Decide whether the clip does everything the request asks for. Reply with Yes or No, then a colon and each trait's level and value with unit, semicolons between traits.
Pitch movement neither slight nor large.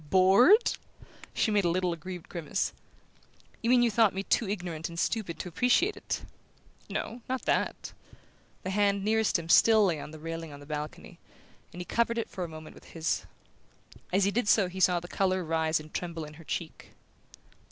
Yes: average, 4.4 semitones